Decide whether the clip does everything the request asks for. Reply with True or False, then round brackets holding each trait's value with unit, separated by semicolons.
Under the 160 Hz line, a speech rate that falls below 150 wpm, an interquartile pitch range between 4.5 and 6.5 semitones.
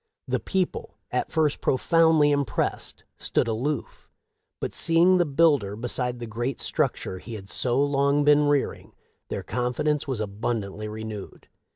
True (135 Hz; 140 wpm; 5.0 semitones)